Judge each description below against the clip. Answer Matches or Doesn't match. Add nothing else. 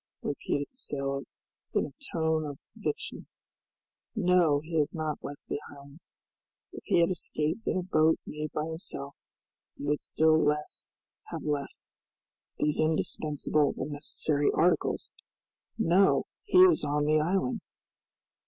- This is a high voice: Doesn't match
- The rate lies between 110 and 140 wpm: Matches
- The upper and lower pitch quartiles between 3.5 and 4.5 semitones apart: Doesn't match